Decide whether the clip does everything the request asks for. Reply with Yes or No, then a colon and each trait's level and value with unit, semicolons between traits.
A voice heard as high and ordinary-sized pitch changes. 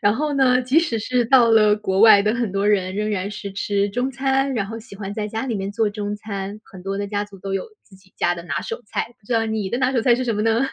Yes: high, 215 Hz; average, 3.3 semitones